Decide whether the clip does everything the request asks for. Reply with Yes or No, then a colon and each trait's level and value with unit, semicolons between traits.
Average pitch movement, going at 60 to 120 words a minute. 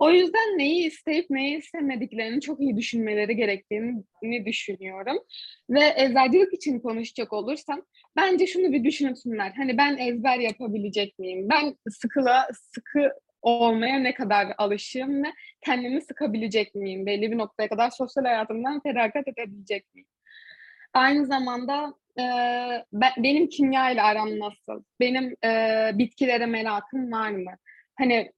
No: average, 4.3 semitones; average, 130 wpm